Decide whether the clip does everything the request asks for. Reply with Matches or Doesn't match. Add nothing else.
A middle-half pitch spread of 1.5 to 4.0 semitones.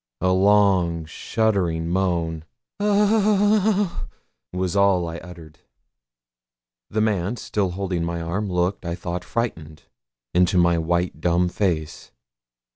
Matches